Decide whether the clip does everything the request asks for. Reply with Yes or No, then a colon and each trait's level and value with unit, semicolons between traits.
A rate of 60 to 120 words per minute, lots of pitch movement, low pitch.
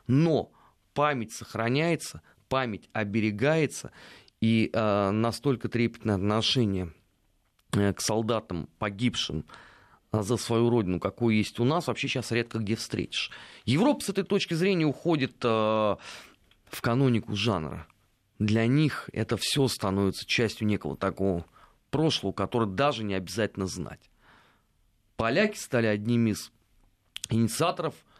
No: average, 115 wpm; average, 3.8 semitones; low, 115 Hz